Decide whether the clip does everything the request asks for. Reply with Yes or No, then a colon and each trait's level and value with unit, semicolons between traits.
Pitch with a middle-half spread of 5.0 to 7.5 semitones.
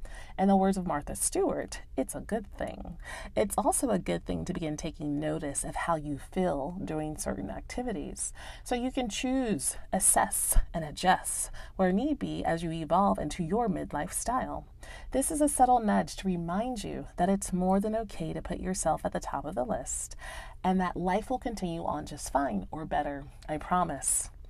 Yes: wide, 5.4 semitones